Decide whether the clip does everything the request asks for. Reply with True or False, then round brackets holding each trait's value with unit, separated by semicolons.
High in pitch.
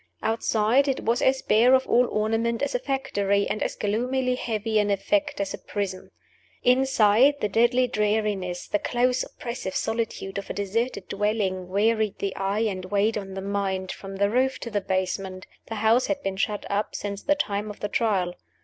True (215 Hz)